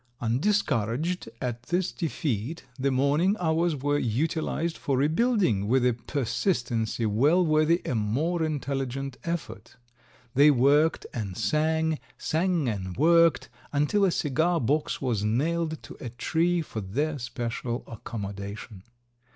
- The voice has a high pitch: No, medium, 145 Hz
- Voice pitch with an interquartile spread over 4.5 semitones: Yes, wide, 5.6 semitones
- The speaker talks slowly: Yes, slow, 125 wpm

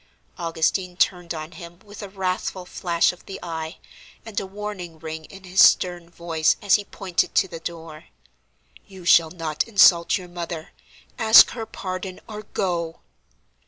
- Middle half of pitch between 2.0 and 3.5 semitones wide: Yes, narrow, 2.5 semitones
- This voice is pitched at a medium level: Yes, medium, 180 Hz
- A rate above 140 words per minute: Yes, average, 160 wpm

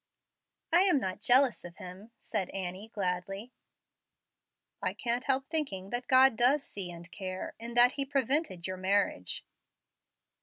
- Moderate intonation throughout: No, wide, 5.9 semitones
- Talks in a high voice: Yes, high, 220 Hz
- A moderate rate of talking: Yes, average, 145 wpm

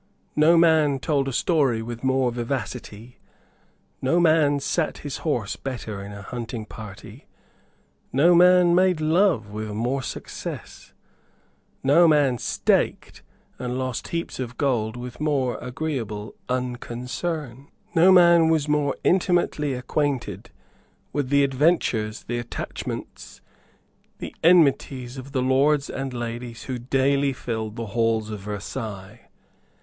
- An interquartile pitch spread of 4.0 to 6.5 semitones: Yes, average, 4.3 semitones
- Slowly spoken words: Yes, slow, 125 wpm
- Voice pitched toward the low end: Yes, low, 130 Hz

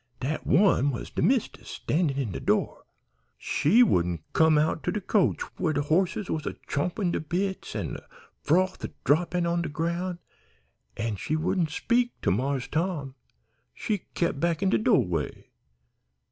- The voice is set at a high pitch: No, medium, 165 Hz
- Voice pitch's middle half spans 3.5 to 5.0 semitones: Yes, average, 4.6 semitones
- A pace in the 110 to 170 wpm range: Yes, average, 165 wpm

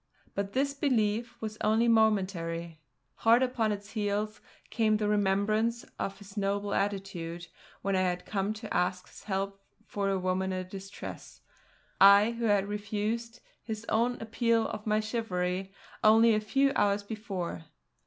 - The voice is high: Yes, high, 205 Hz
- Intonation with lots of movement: No, narrow, 2.4 semitones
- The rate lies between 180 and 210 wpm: No, average, 150 wpm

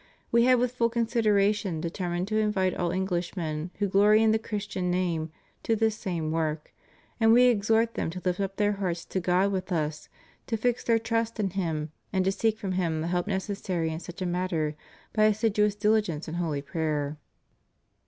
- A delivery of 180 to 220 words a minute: Yes, average, 190 wpm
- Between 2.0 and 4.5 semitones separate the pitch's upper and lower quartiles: Yes, average, 4.1 semitones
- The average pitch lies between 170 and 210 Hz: Yes, high, 190 Hz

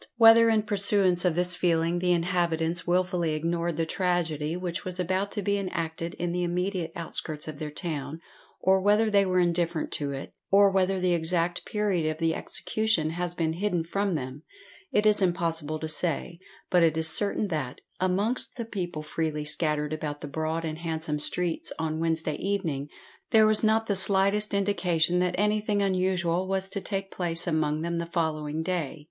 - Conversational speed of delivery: Yes, average, 180 wpm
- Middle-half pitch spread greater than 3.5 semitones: No, average, 3.1 semitones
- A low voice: No, medium, 175 Hz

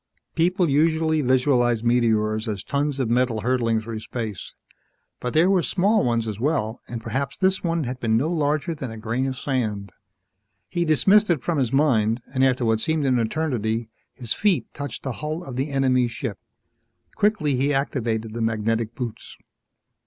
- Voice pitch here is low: Yes, low, 130 Hz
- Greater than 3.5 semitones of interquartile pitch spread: Yes, average, 5.1 semitones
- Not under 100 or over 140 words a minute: No, average, 175 wpm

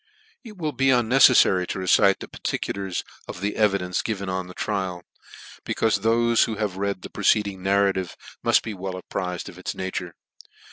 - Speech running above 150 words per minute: Yes, average, 170 wpm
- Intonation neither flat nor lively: Yes, average, 3.1 semitones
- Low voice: Yes, low, 100 Hz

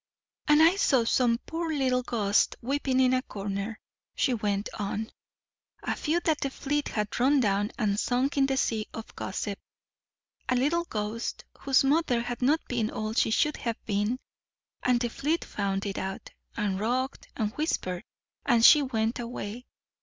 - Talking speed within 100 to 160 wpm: No, average, 170 wpm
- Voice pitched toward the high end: Yes, high, 240 Hz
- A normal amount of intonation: Yes, average, 4.5 semitones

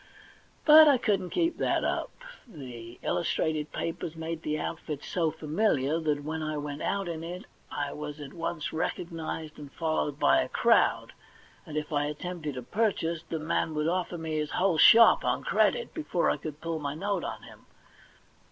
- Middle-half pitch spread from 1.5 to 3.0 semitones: Yes, average, 2.7 semitones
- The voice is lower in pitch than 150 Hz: No, medium, 160 Hz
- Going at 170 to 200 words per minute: Yes, average, 180 wpm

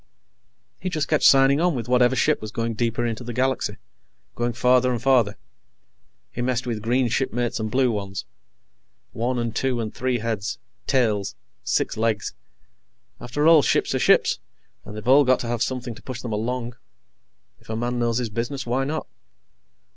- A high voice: No, low, 120 Hz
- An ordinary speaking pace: Yes, average, 175 wpm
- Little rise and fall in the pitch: Yes, narrow, 2.1 semitones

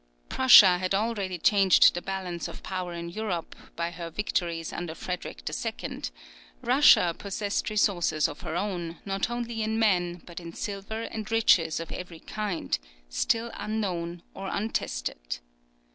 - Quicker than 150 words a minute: No, average, 145 wpm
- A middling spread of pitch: Yes, average, 3.7 semitones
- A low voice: No, medium, 180 Hz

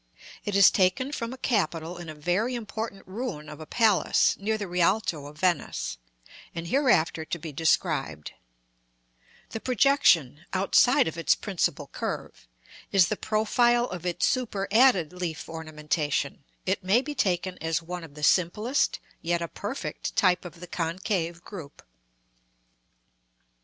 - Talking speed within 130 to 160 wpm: Yes, average, 140 wpm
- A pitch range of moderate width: Yes, average, 5.0 semitones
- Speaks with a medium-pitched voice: Yes, medium, 180 Hz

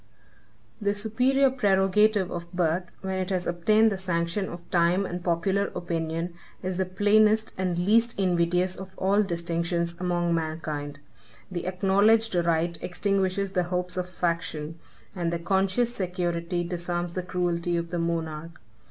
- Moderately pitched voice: Yes, medium, 180 Hz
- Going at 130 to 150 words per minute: Yes, average, 145 wpm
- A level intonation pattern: Yes, narrow, 2.3 semitones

